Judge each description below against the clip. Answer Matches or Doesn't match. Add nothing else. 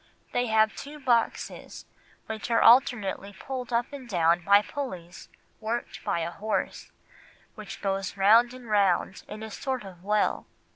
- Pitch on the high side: Matches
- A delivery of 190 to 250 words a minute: Doesn't match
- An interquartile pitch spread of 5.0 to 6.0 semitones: Doesn't match